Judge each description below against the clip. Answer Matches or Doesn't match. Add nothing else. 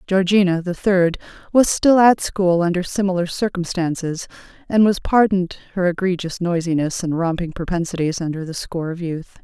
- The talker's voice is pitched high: Doesn't match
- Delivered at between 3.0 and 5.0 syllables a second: Doesn't match